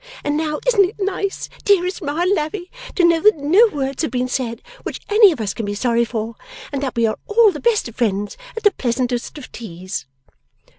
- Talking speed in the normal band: No, fast, 215 wpm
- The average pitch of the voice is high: Yes, very high, 290 Hz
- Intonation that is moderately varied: No, wide, 8.5 semitones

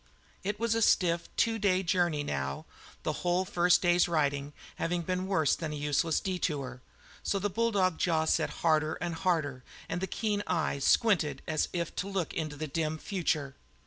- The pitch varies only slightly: No, average, 3.5 semitones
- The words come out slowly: No, average, 175 wpm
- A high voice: No, medium, 170 Hz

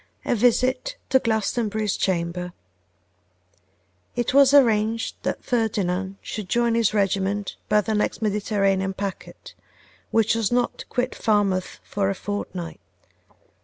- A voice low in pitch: No, high, 210 Hz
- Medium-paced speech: No, slow, 125 wpm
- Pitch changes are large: No, average, 3.1 semitones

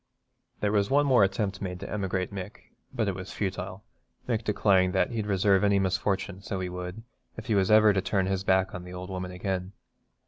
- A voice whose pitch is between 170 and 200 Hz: No, very low, 95 Hz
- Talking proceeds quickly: Yes, fast, 210 wpm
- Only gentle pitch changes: Yes, narrow, 1.9 semitones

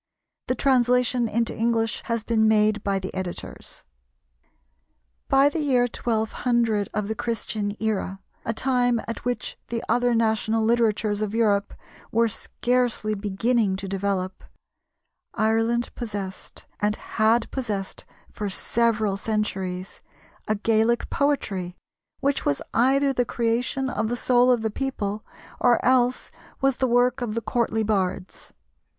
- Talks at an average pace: No, slow, 130 wpm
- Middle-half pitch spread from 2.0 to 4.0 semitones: Yes, average, 2.7 semitones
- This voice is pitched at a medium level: No, high, 225 Hz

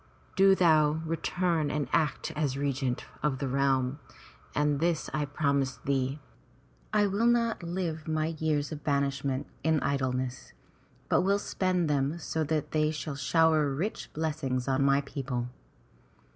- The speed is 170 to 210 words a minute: No, average, 145 wpm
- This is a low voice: No, medium, 150 Hz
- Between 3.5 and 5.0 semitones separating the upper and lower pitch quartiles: No, average, 2.9 semitones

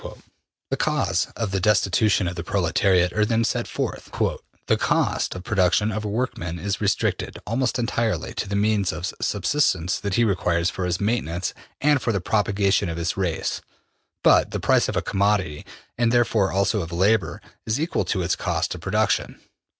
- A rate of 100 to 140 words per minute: No, average, 180 wpm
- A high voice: No, low, 100 Hz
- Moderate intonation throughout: Yes, average, 3.4 semitones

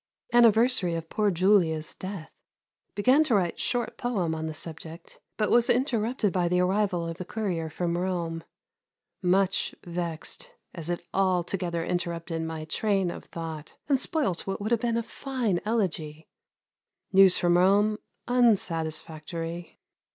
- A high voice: No, medium, 180 Hz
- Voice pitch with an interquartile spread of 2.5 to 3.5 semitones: No, average, 4.3 semitones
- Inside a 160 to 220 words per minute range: No, average, 140 wpm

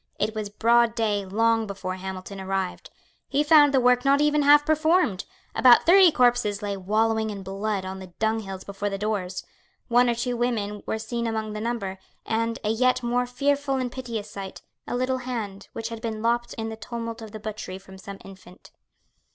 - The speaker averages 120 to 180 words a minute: No, average, 190 wpm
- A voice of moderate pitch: No, high, 225 Hz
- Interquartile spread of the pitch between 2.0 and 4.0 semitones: Yes, average, 3.5 semitones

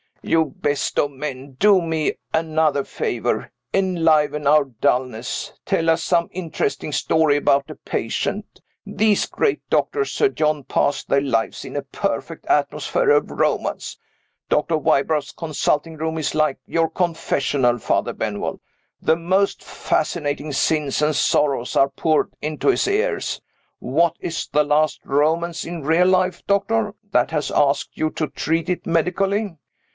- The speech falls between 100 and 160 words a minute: Yes, average, 140 wpm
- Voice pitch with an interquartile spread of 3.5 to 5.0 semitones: No, average, 2.9 semitones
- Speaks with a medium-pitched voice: Yes, medium, 155 Hz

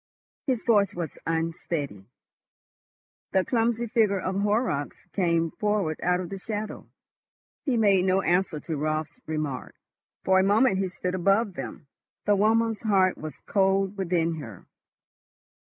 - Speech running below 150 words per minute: Yes, average, 140 wpm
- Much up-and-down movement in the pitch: No, average, 4.1 semitones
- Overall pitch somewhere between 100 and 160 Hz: No, high, 190 Hz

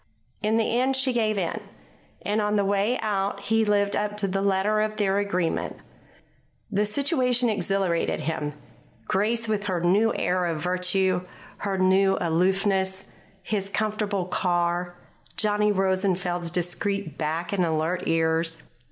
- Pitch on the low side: No, high, 195 Hz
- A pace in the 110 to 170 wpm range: Yes, average, 140 wpm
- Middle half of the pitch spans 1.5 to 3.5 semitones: Yes, average, 2.9 semitones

